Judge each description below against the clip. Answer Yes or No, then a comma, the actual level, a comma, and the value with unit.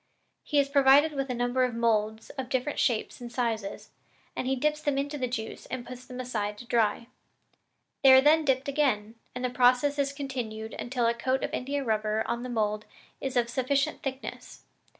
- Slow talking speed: No, average, 195 wpm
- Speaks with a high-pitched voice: Yes, very high, 255 Hz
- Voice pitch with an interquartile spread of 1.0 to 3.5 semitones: Yes, average, 2.8 semitones